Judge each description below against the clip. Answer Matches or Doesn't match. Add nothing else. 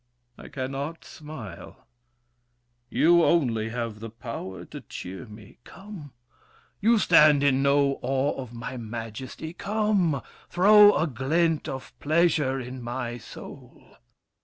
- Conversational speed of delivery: Doesn't match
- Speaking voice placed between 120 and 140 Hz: Matches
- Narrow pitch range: Doesn't match